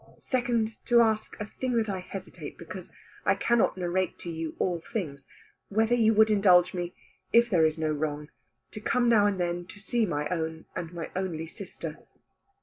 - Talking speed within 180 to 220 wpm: Yes, average, 185 wpm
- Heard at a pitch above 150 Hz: Yes, medium, 185 Hz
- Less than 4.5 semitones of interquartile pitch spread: No, average, 4.9 semitones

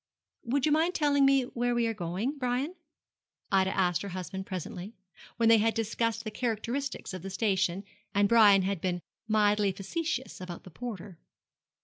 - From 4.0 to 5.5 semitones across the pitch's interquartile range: Yes, average, 4.4 semitones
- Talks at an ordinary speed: Yes, average, 165 wpm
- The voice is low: No, high, 215 Hz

